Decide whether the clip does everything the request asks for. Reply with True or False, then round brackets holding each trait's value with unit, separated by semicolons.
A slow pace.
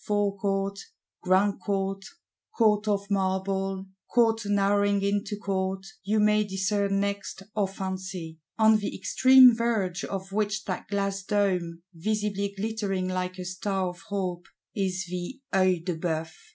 True (130 wpm)